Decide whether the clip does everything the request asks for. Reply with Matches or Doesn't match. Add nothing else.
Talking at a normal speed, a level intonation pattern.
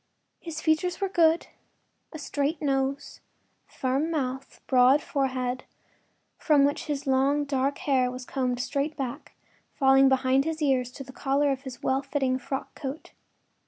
Matches